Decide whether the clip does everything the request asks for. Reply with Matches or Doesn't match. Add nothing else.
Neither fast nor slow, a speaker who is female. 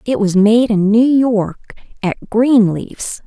Matches